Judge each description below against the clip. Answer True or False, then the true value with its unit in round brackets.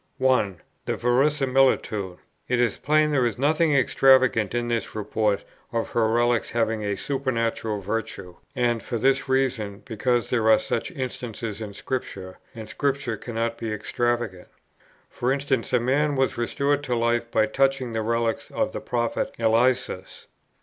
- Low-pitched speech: True (120 Hz)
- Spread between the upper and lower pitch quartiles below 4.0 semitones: True (2.9 semitones)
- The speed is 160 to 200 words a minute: False (150 wpm)